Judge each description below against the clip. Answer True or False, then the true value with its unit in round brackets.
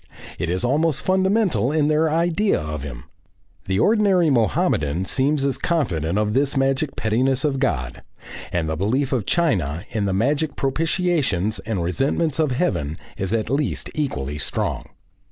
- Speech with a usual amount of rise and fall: False (8.5 semitones)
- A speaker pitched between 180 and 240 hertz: False (130 Hz)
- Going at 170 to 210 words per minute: False (155 wpm)